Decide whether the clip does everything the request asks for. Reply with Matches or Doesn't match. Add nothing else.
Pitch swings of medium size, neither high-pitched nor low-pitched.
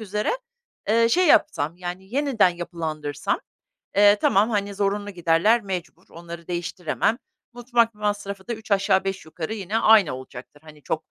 Doesn't match